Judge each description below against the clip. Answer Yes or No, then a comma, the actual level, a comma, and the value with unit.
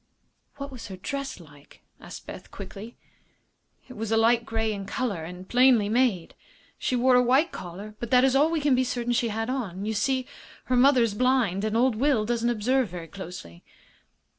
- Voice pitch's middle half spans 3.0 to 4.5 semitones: Yes, average, 4.0 semitones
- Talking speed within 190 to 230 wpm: Yes, average, 195 wpm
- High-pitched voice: Yes, high, 230 Hz